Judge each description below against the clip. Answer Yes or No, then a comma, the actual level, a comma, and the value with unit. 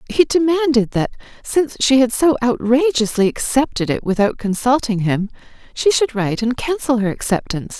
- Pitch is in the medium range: No, high, 245 Hz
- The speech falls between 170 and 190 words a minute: No, average, 155 wpm